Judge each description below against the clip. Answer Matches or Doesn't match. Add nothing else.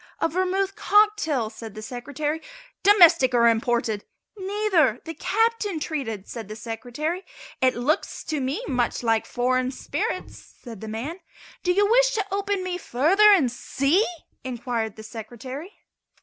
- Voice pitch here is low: Doesn't match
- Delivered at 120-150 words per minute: Matches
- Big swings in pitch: Matches